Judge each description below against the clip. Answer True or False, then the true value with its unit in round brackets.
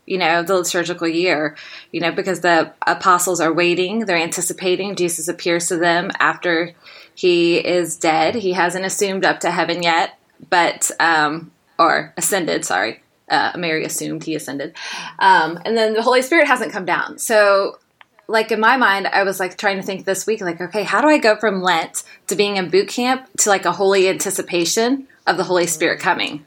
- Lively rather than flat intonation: False (3.2 semitones)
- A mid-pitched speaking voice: True (180 Hz)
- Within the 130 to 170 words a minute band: False (190 wpm)